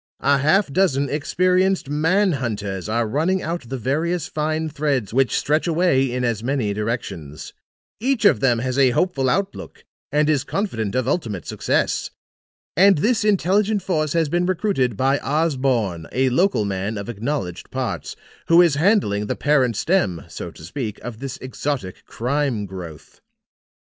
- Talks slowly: No, average, 155 wpm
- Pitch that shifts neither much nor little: No, wide, 6.7 semitones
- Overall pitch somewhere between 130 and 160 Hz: Yes, medium, 140 Hz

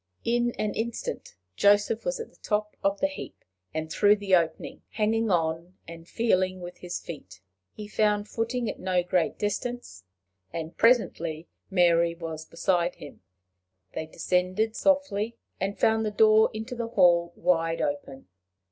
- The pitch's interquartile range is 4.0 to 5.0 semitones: Yes, average, 4.6 semitones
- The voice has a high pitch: Yes, high, 195 Hz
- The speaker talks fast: No, average, 150 wpm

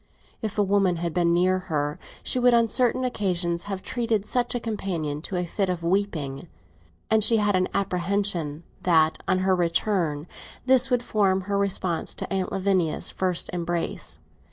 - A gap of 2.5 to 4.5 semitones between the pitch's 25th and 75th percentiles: Yes, average, 3.4 semitones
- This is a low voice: No, high, 190 Hz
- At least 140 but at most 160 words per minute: No, average, 170 wpm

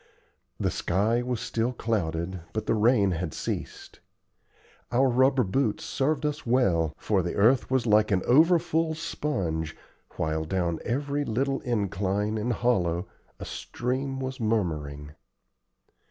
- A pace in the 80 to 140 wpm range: Yes, slow, 135 wpm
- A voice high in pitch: No, low, 115 Hz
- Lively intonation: Yes, wide, 6.2 semitones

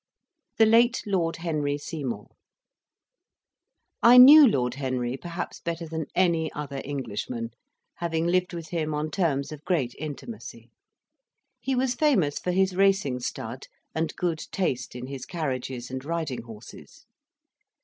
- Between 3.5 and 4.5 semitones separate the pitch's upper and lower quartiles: No, average, 5.2 semitones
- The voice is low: No, medium, 160 Hz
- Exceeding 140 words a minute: No, slow, 135 wpm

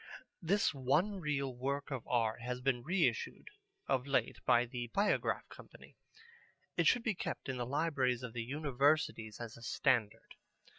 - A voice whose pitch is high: No, low, 130 Hz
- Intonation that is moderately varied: Yes, average, 3.8 semitones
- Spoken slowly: No, average, 155 wpm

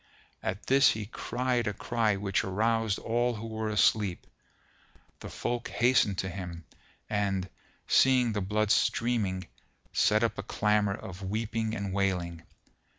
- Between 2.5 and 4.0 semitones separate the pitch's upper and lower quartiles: Yes, average, 2.9 semitones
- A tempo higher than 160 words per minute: No, average, 140 wpm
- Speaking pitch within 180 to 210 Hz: No, low, 105 Hz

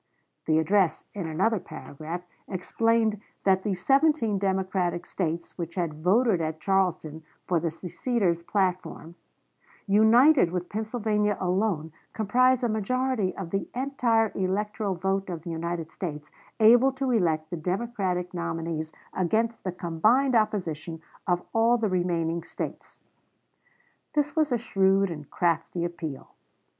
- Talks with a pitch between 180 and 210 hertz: Yes, high, 190 Hz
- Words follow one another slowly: Yes, slow, 130 wpm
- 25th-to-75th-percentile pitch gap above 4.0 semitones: Yes, average, 4.7 semitones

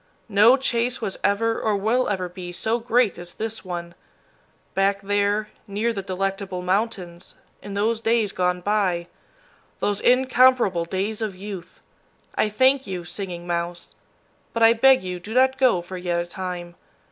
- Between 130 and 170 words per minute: Yes, average, 160 wpm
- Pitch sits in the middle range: No, high, 200 Hz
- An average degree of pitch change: Yes, average, 4.1 semitones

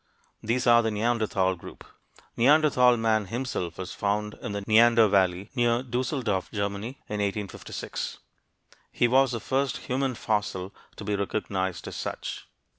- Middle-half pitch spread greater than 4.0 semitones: No, average, 3.4 semitones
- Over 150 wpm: No, average, 140 wpm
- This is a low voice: Yes, low, 110 Hz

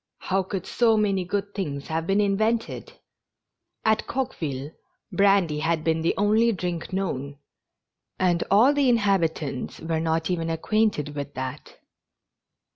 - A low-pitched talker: No, medium, 180 Hz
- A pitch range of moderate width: Yes, average, 4.4 semitones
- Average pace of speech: No, slow, 130 wpm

